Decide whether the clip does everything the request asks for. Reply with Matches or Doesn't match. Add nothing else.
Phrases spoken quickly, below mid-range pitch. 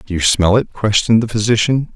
Matches